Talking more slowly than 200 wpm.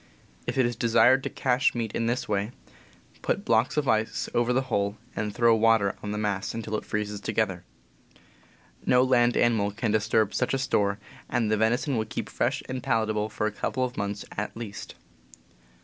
Yes: average, 190 wpm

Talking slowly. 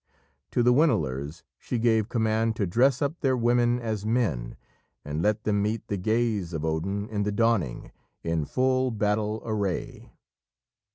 No: average, 155 wpm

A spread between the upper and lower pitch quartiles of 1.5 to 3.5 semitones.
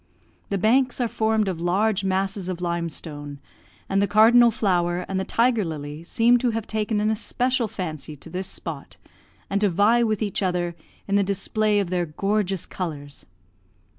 No: average, 3.9 semitones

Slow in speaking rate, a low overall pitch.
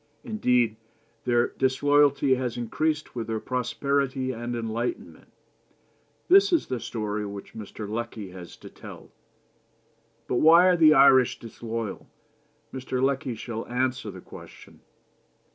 Yes: slow, 125 wpm; low, 125 Hz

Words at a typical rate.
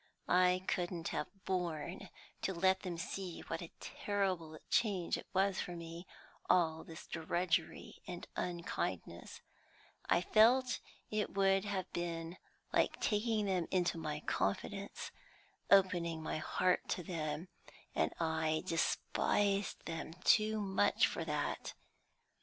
No: slow, 125 wpm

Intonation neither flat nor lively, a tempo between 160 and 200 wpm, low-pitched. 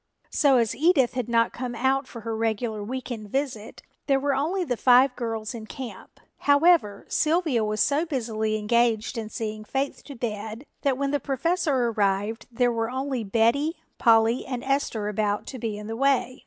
No: average, 3.7 semitones; average, 180 wpm; high, 240 Hz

